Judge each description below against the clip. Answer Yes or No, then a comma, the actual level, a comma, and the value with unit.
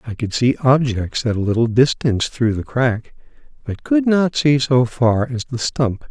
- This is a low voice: Yes, low, 125 Hz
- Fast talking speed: No, average, 195 wpm